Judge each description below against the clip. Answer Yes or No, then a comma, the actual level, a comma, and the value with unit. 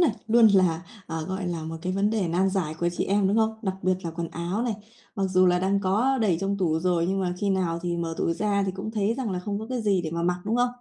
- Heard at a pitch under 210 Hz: Yes, high, 190 Hz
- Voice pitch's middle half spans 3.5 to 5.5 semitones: No, average, 3.1 semitones